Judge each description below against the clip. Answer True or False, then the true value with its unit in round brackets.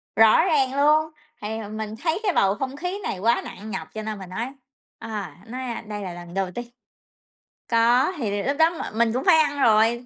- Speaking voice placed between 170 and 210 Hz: False (230 Hz)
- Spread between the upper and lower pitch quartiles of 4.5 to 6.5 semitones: True (5.1 semitones)